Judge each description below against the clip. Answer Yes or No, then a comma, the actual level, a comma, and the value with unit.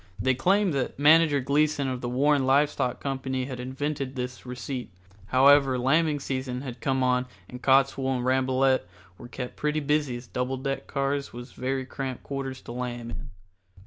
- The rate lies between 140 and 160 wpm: No, average, 175 wpm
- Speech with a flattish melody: Yes, narrow, 1.8 semitones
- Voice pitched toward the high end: No, low, 130 Hz